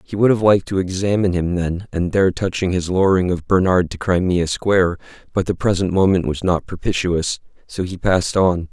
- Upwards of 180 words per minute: Yes, average, 200 wpm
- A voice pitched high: No, very low, 90 Hz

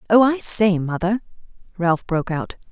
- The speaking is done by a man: No, female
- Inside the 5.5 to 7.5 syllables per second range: No, 4.8 syllables/s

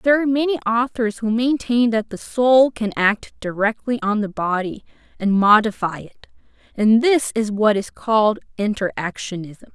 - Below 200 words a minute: Yes, average, 160 wpm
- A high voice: Yes, high, 220 Hz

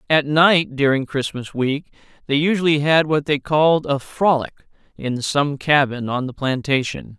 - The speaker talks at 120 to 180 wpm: Yes, average, 160 wpm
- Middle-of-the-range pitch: Yes, medium, 145 Hz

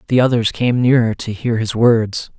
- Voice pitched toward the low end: Yes, low, 115 Hz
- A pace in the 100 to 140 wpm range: No, average, 200 wpm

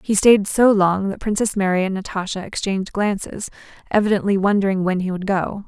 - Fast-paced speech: No, average, 180 wpm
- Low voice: No, high, 195 Hz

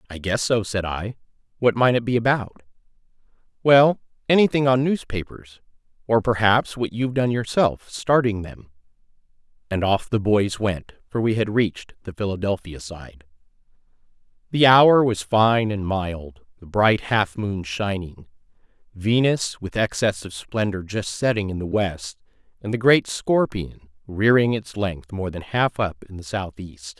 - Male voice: Yes, male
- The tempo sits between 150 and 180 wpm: Yes, average, 155 wpm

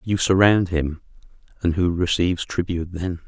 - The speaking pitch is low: Yes, very low, 90 Hz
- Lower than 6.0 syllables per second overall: Yes, 5.1 syllables/s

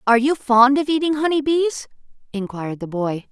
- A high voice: Yes, very high, 255 Hz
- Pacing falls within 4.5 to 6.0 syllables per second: Yes, 5.5 syllables/s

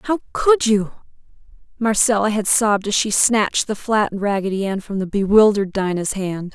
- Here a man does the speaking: No, female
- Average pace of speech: Yes, average, 165 wpm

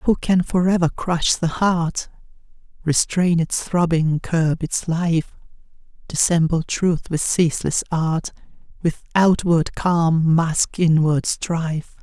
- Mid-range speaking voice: Yes, medium, 165 Hz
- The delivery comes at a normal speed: No, slow, 120 wpm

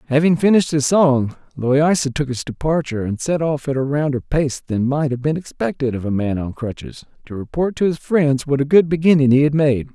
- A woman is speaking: No, male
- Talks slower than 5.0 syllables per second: No, 5.5 syllables/s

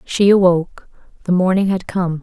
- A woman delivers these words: Yes, female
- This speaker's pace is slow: No, average, 160 wpm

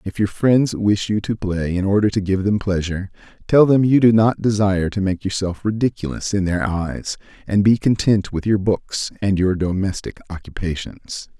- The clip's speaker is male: Yes, male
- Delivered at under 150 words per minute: No, average, 190 wpm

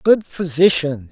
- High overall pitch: No, medium, 160 Hz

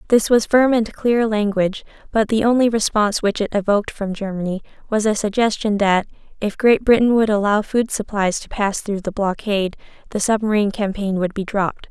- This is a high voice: Yes, high, 210 Hz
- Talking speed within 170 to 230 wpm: Yes, average, 185 wpm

